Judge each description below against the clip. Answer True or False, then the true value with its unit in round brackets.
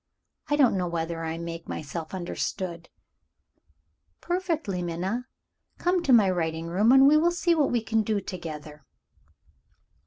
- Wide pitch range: True (8.2 semitones)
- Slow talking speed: False (145 wpm)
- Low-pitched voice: False (190 Hz)